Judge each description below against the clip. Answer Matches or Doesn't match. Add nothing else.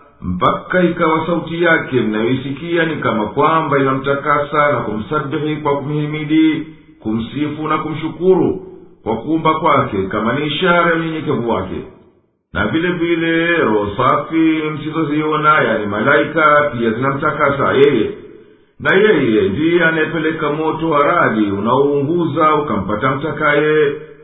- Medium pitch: Matches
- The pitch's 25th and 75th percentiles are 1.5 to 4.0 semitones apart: Matches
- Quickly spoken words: Doesn't match